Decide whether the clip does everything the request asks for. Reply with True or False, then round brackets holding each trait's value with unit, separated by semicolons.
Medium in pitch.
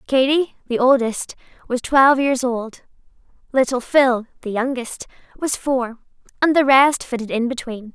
False (255 Hz)